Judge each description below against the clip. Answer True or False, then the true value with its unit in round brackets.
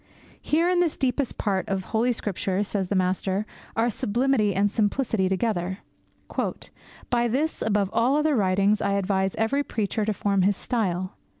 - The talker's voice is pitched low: False (210 Hz)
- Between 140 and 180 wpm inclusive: True (160 wpm)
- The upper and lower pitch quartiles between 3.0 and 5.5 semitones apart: True (3.8 semitones)